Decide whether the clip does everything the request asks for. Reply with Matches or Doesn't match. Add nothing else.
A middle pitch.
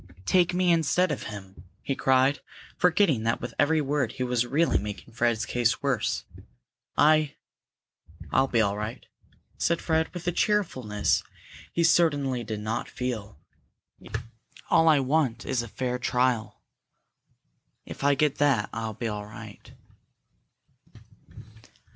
Doesn't match